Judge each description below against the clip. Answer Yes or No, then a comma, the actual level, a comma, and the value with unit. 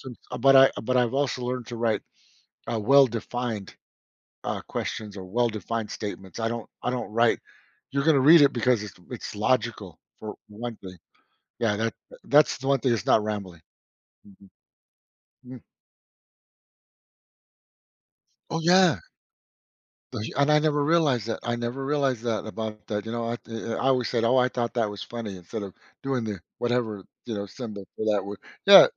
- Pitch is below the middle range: Yes, low, 115 Hz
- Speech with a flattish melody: No, average, 3.3 semitones